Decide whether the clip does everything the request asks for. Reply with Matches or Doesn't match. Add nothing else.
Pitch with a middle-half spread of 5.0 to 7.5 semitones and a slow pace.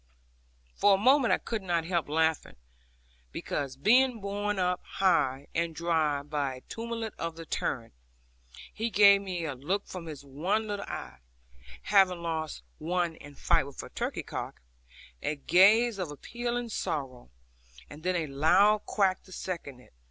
Doesn't match